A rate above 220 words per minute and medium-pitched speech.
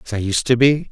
No: fast, 330 wpm; low, 115 Hz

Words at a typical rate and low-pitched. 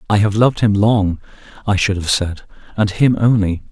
Yes: average, 195 wpm; low, 100 Hz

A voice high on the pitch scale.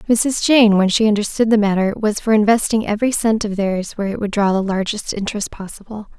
Yes: high, 210 Hz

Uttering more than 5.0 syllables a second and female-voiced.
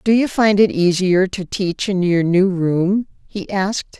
No: 4.1 syllables/s; female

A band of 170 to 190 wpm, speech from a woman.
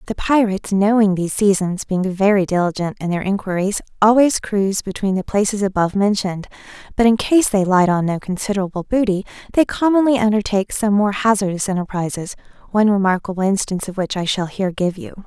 Yes: average, 175 wpm; female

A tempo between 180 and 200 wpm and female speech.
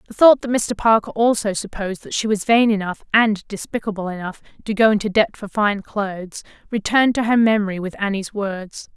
Yes: average, 195 wpm; female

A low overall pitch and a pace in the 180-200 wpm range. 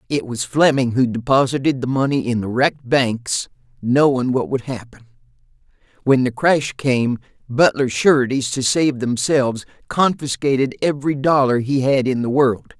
No: low, 130 Hz; average, 150 wpm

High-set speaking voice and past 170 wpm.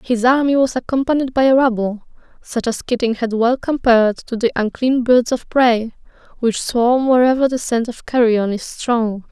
Yes: high, 240 Hz; average, 180 wpm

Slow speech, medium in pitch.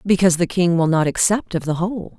No: fast, 245 wpm; medium, 175 Hz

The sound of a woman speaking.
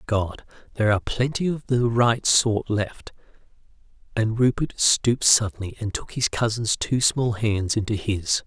No: male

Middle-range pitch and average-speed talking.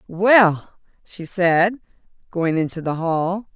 No: medium, 180 Hz; slow, 120 wpm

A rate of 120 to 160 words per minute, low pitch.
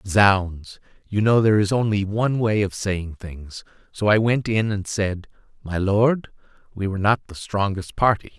No: average, 170 wpm; low, 105 Hz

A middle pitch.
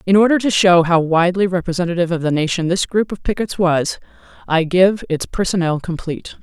Yes: medium, 175 Hz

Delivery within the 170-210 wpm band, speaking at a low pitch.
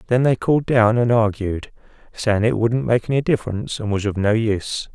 Yes: fast, 205 wpm; low, 110 Hz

